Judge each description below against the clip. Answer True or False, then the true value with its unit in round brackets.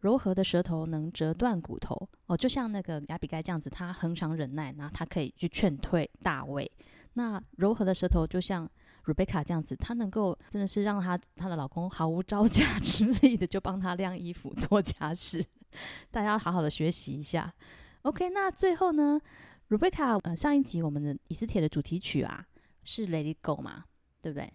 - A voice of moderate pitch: True (180 Hz)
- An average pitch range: True (4.7 semitones)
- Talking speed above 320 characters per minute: False (300 characters per minute)